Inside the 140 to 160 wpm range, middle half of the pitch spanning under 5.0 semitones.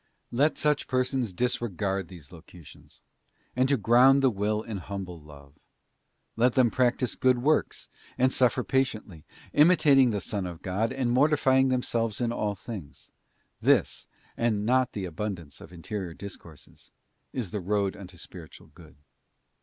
No: average, 155 wpm; wide, 5.6 semitones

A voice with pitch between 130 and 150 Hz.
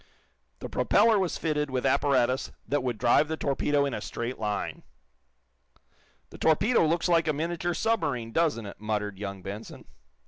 Yes: medium, 140 Hz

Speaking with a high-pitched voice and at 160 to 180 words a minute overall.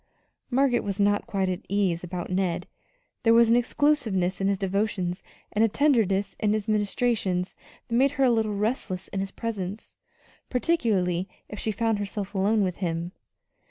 Yes: high, 205 Hz; average, 165 wpm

